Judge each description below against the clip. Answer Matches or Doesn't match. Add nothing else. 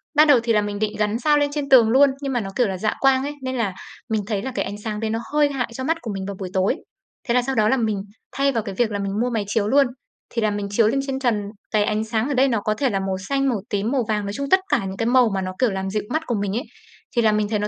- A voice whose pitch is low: Doesn't match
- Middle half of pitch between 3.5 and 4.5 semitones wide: Matches